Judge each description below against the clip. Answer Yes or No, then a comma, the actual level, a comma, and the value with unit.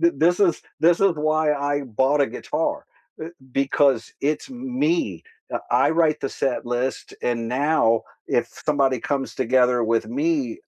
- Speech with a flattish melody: No, average, 4.5 semitones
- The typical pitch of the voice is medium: Yes, medium, 145 Hz